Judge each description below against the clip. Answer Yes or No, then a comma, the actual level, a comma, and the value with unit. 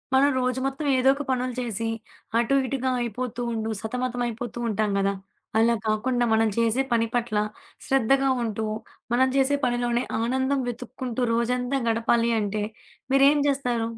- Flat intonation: Yes, narrow, 2.3 semitones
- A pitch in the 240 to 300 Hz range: Yes, high, 245 Hz